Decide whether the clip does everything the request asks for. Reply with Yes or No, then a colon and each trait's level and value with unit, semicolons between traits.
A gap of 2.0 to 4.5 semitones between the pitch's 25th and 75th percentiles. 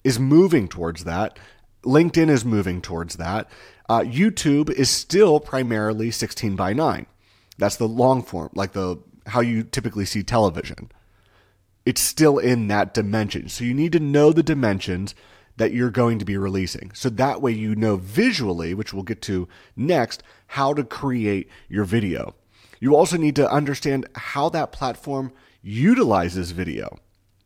No: wide, 5.4 semitones